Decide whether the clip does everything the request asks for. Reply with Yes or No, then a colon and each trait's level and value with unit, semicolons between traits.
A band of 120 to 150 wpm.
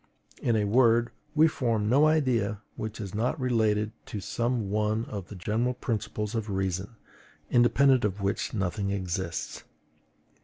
Yes: average, 145 wpm